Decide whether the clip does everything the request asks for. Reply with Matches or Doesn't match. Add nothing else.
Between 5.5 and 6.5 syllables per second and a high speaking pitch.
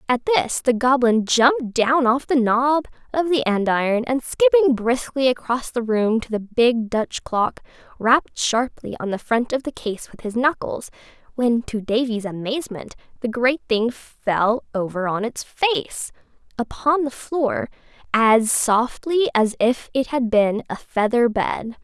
Doesn't match